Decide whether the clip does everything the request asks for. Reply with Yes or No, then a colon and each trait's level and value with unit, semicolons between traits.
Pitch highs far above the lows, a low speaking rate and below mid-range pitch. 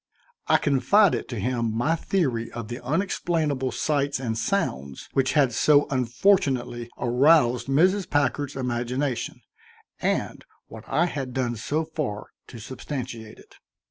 No: average, 4.0 semitones; slow, 130 wpm; low, 130 Hz